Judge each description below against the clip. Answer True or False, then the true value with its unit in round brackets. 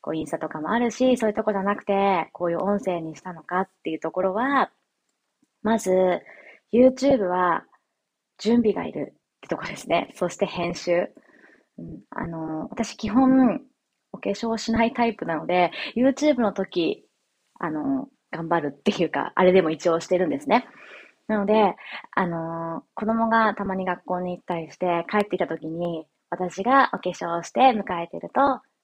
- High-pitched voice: True (200 Hz)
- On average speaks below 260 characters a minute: False (330 characters per minute)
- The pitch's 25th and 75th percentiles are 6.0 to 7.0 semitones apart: False (5.5 semitones)